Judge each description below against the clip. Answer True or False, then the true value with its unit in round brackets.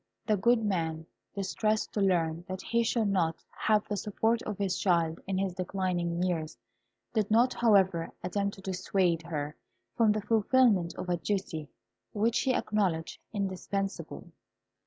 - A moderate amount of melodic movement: True (3.6 semitones)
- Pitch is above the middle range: True (195 Hz)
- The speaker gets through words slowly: False (150 wpm)